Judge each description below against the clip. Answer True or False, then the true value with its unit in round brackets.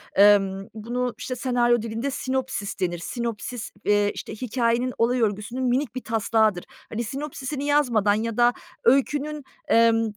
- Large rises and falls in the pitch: False (3.1 semitones)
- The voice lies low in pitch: False (235 Hz)